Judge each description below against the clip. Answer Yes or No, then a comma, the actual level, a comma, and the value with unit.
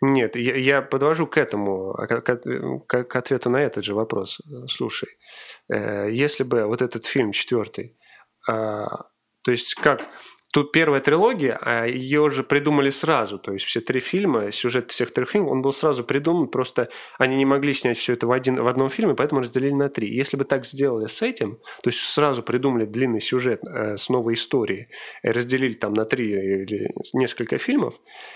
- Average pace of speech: No, fast, 165 wpm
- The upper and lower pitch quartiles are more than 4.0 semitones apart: No, average, 3.3 semitones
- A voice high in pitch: No, low, 130 Hz